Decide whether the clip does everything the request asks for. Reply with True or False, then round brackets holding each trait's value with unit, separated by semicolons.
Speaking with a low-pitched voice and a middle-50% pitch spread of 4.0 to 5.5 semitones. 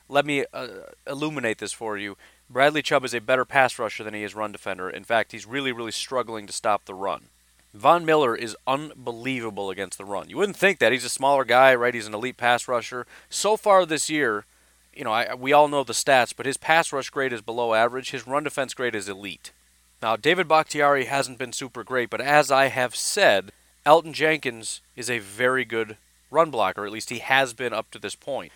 True (125 Hz; 4.4 semitones)